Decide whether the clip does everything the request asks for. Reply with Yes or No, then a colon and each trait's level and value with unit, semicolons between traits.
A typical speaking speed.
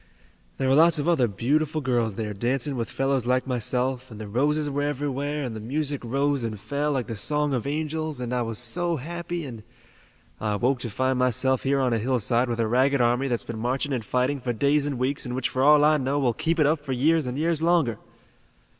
No: fast, 230 wpm